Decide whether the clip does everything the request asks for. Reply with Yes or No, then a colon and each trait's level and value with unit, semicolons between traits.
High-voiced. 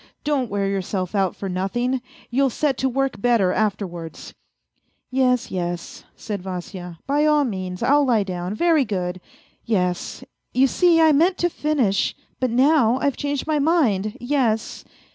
Yes: high, 235 Hz